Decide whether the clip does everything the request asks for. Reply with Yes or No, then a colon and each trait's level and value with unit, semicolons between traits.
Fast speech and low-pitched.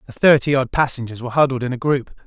Yes: fast, 240 wpm; low, 130 Hz